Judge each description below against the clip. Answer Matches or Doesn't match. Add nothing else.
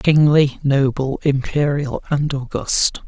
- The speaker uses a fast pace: Doesn't match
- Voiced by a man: Matches